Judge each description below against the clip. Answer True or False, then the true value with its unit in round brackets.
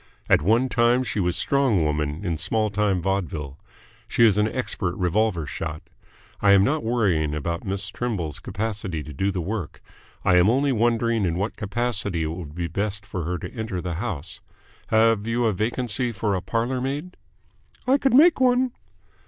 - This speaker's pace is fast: False (185 wpm)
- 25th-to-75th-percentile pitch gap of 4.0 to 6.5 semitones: True (5.2 semitones)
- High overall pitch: False (105 Hz)